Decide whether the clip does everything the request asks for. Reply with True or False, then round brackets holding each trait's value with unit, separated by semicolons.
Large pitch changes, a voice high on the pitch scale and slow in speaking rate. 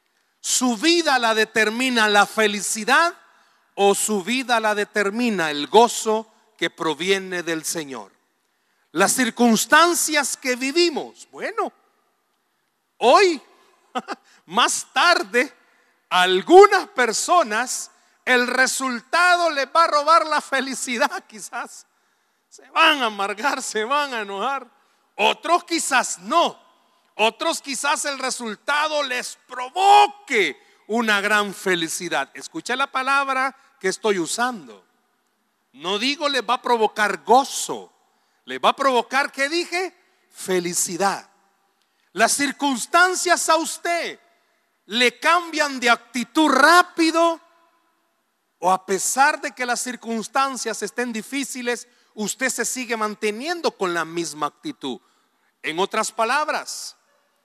True (7.4 semitones; 255 Hz; 110 wpm)